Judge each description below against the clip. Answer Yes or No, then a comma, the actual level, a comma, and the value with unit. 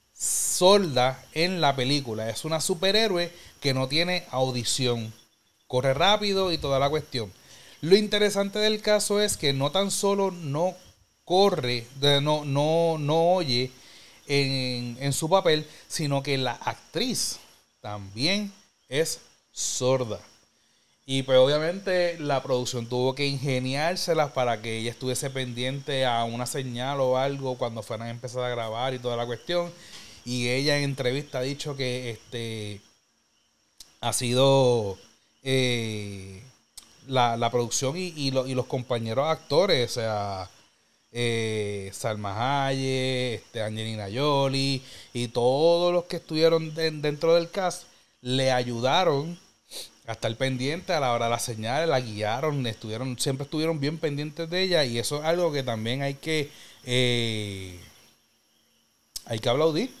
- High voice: No, low, 130 Hz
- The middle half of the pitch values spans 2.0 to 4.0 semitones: No, average, 4.8 semitones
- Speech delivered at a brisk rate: No, average, 140 wpm